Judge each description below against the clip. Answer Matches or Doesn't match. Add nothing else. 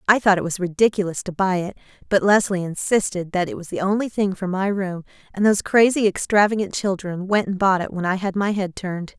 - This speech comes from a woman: Matches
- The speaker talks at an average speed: Doesn't match